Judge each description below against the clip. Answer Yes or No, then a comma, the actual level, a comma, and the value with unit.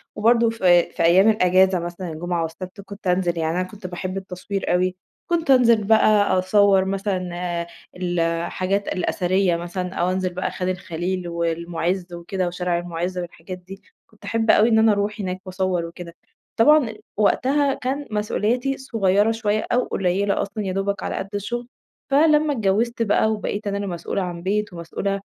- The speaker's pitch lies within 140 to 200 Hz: Yes, high, 190 Hz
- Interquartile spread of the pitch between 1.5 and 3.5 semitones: Yes, average, 3.1 semitones